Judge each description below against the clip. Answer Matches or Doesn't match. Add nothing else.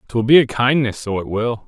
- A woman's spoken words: Doesn't match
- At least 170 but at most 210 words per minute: Doesn't match